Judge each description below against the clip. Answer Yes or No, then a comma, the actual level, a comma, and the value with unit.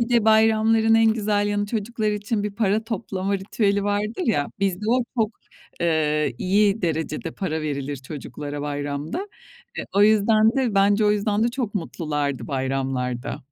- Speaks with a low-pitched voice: No, high, 205 Hz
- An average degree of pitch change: No, wide, 6.3 semitones